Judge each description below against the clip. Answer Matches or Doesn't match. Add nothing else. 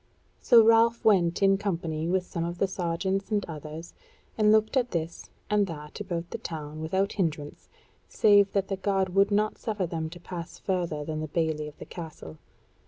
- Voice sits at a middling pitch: Matches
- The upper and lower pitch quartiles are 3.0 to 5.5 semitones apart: Matches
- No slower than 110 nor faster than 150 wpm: Doesn't match